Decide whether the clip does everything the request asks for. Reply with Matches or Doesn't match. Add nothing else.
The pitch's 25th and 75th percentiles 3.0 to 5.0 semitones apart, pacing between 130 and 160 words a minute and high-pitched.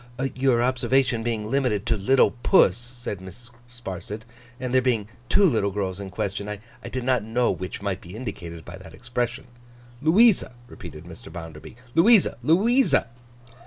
Doesn't match